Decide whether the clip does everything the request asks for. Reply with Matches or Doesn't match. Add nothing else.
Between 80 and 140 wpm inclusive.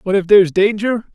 Doesn't match